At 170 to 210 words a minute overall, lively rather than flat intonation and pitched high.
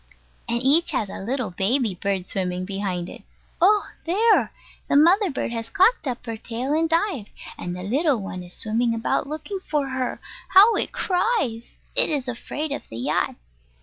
Yes: average, 175 wpm; wide, 8.3 semitones; very high, 255 Hz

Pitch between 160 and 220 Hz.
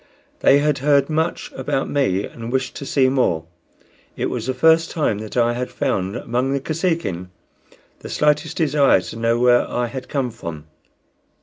No: low, 130 Hz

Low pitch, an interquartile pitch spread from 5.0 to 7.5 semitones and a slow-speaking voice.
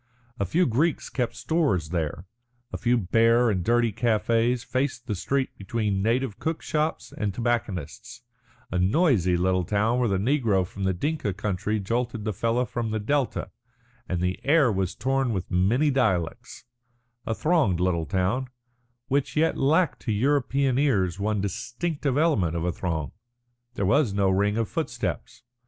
No: low, 115 Hz; wide, 5.6 semitones; average, 160 wpm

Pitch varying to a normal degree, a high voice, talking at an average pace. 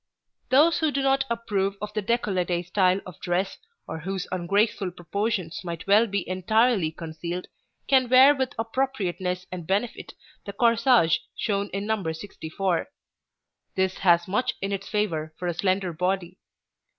Yes: average, 4.1 semitones; high, 195 Hz; average, 150 wpm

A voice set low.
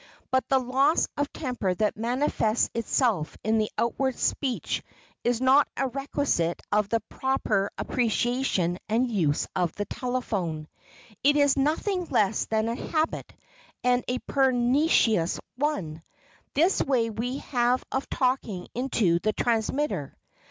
No: high, 245 Hz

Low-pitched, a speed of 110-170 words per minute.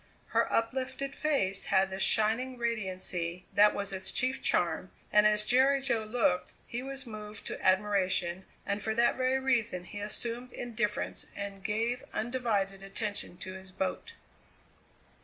No: high, 210 Hz; average, 145 wpm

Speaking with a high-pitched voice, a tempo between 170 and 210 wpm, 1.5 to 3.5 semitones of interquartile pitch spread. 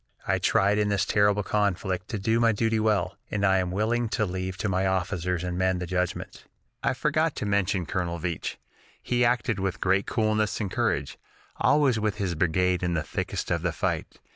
No: low, 100 Hz; average, 195 wpm; average, 2.9 semitones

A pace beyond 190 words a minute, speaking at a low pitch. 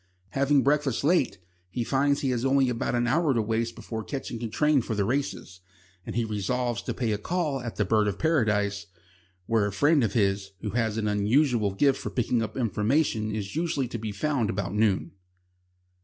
Yes: average, 200 wpm; low, 115 Hz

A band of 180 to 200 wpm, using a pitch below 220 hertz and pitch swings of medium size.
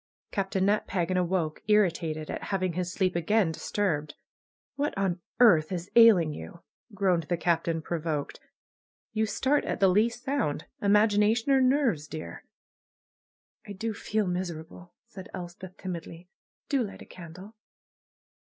No: average, 140 wpm; medium, 185 Hz; average, 3.9 semitones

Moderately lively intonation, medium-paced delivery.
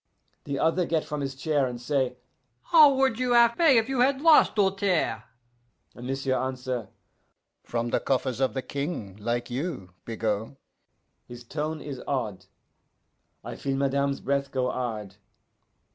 No: wide, 6.0 semitones; average, 150 wpm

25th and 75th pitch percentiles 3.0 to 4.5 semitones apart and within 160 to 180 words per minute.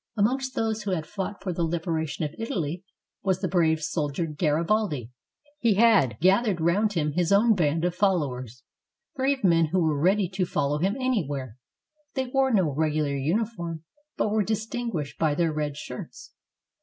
No: wide, 5.6 semitones; average, 170 wpm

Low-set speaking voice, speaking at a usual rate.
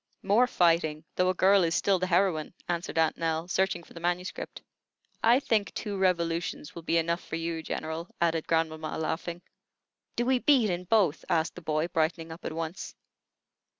No: medium, 170 Hz; average, 180 wpm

